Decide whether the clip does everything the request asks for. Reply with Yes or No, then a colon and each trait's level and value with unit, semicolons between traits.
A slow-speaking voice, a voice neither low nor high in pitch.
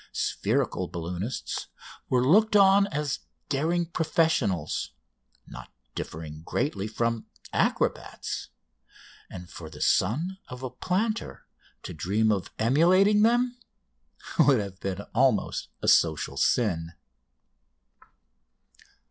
No: slow, 100 wpm; low, 125 Hz